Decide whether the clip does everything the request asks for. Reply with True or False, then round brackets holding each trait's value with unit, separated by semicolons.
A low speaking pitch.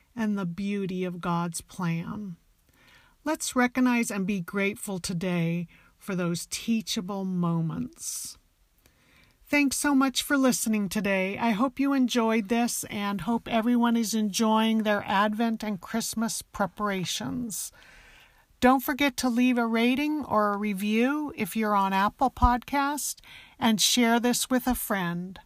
False (220 Hz)